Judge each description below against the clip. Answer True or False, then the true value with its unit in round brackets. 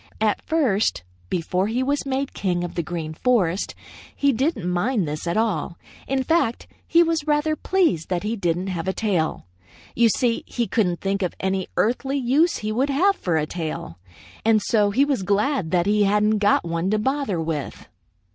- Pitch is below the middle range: False (210 Hz)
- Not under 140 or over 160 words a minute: False (185 wpm)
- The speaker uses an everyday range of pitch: False (7.0 semitones)